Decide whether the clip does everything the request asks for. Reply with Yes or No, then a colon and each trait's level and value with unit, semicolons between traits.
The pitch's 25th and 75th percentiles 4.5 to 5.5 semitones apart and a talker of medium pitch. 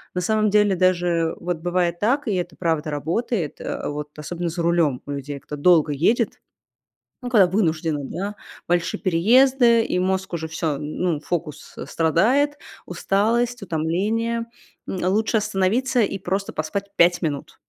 Yes: average, 4.9 semitones; medium, 180 Hz